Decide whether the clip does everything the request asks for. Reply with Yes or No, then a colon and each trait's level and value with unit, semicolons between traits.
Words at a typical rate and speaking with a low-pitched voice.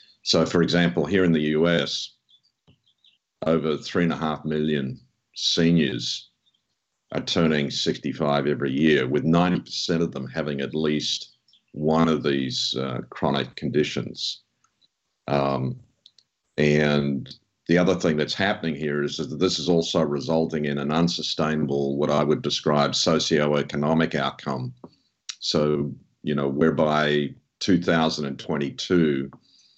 No: slow, 120 wpm; very low, 75 Hz